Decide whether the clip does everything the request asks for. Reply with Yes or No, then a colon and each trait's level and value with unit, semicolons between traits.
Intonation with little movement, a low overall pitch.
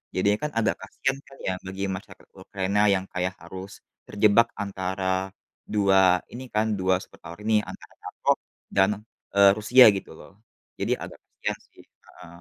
Yes: narrow, 2.2 semitones; low, 100 Hz